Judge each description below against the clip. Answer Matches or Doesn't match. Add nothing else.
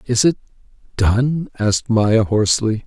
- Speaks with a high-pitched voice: Doesn't match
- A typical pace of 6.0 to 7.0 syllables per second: Doesn't match